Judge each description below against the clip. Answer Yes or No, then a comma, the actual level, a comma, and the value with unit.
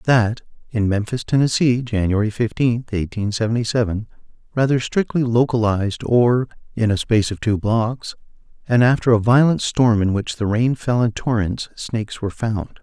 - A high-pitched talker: No, low, 115 Hz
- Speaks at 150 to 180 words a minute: Yes, average, 160 wpm